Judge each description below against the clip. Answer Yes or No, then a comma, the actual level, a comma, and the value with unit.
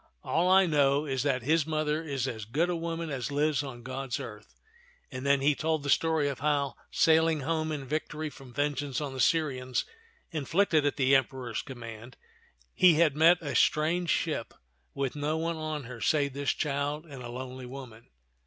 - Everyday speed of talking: Yes, average, 190 wpm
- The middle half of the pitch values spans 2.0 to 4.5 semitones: Yes, average, 3.1 semitones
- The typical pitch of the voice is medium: Yes, medium, 145 Hz